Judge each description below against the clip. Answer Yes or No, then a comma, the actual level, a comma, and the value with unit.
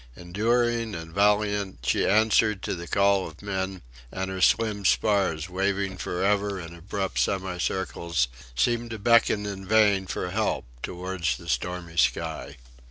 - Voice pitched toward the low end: Yes, very low, 95 Hz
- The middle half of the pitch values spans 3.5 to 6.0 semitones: No, narrow, 2.5 semitones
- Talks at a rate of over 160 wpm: No, average, 145 wpm